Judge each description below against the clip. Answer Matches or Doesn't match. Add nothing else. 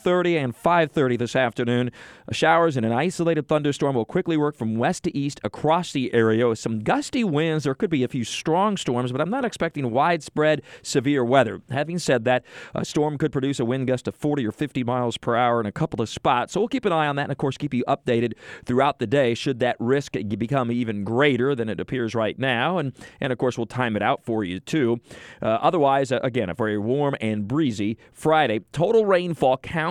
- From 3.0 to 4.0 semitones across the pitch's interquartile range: Doesn't match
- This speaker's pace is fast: Matches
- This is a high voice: Doesn't match